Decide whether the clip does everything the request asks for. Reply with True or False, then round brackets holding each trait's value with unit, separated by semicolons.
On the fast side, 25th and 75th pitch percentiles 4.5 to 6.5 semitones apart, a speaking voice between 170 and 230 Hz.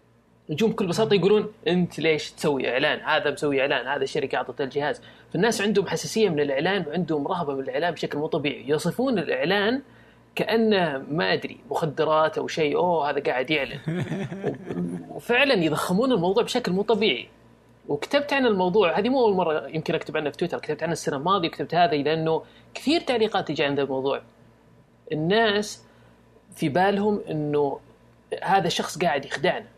True (155 wpm; 5.5 semitones; 175 Hz)